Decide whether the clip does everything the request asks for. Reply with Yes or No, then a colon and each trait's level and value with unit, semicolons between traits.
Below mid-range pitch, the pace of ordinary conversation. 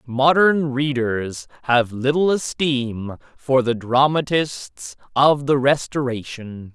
No: low, 130 Hz; slow, 100 wpm